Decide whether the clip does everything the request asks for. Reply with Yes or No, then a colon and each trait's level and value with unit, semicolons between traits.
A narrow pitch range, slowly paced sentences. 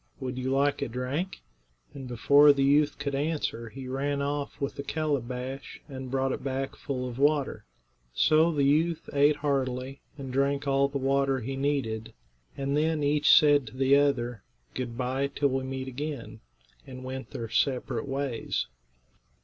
No: narrow, 1.8 semitones; average, 165 wpm